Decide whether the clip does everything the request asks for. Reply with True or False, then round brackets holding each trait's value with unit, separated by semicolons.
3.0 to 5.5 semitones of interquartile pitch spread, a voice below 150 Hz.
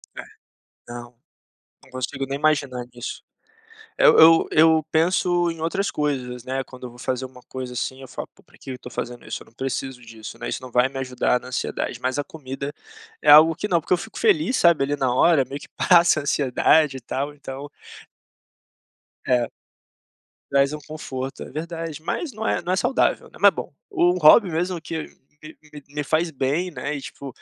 True (4.0 semitones; 140 Hz)